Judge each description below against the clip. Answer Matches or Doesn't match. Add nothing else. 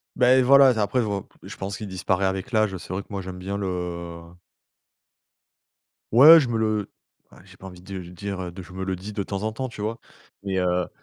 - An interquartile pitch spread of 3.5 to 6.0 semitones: Doesn't match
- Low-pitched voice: Matches